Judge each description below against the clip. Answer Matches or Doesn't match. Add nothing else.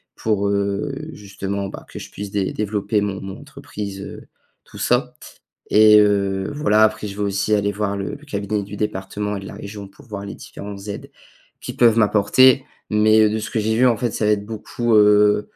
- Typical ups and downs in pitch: Doesn't match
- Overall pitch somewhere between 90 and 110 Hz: Matches